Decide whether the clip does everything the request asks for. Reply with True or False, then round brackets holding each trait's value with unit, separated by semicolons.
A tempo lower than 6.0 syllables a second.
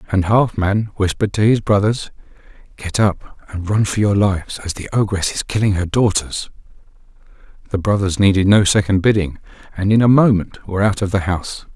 True (5.5 syllables/s)